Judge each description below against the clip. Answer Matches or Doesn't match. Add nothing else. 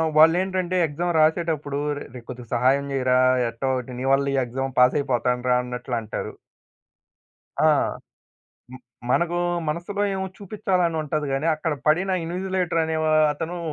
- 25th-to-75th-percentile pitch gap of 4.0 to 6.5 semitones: Matches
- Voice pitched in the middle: Matches